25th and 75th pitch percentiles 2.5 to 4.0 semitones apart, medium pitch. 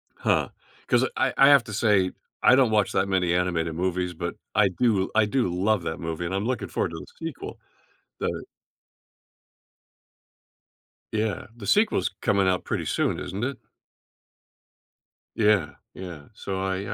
No: average, 3.3 semitones; very low, 95 Hz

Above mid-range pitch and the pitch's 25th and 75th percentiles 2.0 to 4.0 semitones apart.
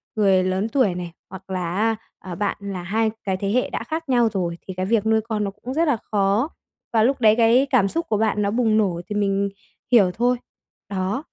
Yes: high, 210 Hz; average, 3.3 semitones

